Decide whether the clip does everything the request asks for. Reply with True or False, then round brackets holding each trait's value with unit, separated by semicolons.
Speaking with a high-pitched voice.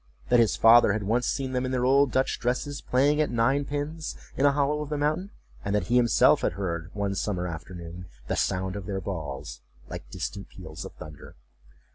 False (120 Hz)